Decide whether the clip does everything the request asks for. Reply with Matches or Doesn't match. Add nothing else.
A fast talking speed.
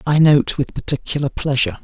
Doesn't match